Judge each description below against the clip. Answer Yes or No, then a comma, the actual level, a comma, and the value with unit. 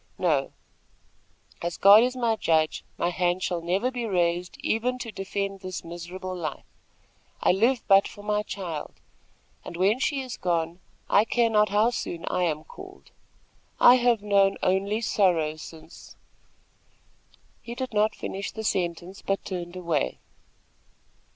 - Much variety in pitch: No, average, 4.2 semitones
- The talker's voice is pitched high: Yes, high, 195 Hz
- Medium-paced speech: Yes, average, 150 wpm